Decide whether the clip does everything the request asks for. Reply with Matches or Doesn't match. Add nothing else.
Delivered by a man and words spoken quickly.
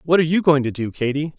Matches